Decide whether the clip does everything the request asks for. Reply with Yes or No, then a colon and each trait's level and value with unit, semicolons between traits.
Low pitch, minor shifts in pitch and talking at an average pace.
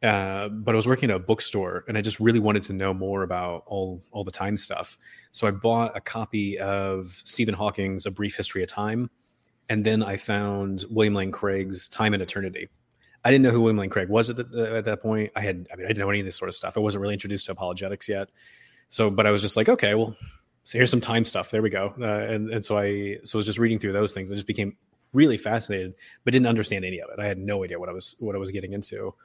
No: low, 105 Hz; narrow, 2.1 semitones; fast, 270 wpm